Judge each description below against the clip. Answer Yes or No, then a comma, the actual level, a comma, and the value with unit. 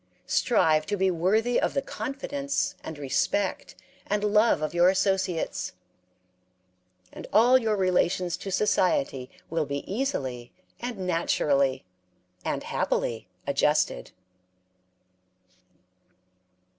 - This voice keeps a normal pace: No, slow, 100 wpm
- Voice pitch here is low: No, medium, 185 Hz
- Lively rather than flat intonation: Yes, wide, 6.1 semitones